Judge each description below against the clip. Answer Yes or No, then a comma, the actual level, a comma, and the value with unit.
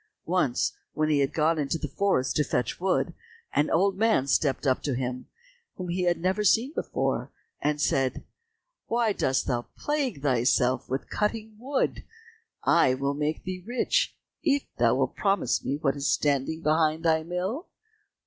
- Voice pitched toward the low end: No, medium, 160 Hz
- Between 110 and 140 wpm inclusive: No, average, 165 wpm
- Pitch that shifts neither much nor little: No, wide, 6.1 semitones